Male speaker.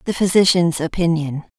No: female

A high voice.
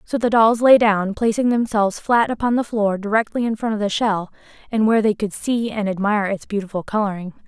Yes: high, 215 Hz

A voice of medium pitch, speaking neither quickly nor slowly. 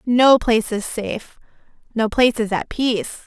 No: high, 230 Hz; average, 145 wpm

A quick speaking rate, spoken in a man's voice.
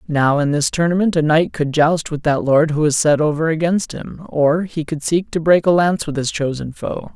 Yes: fast, 245 wpm; male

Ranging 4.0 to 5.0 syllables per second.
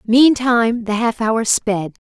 No: 3.7 syllables/s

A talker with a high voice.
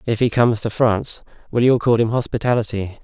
No: low, 115 Hz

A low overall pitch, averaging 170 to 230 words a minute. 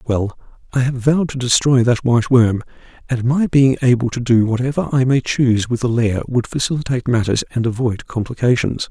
Yes: low, 125 Hz; average, 190 wpm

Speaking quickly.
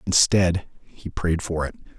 No: average, 150 wpm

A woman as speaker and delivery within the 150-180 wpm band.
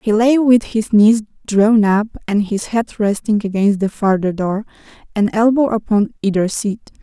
Yes: female; average, 170 wpm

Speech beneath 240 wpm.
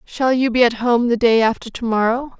No: fast, 250 wpm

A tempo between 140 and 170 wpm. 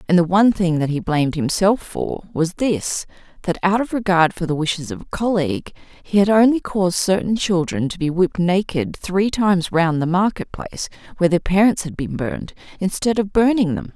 No: average, 200 wpm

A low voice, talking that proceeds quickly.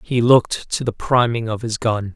Yes: low, 115 Hz; fast, 225 wpm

